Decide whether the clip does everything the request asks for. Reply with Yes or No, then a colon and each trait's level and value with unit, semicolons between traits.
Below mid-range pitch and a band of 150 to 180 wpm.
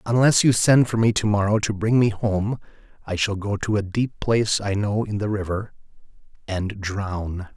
No: low, 105 Hz; average, 200 wpm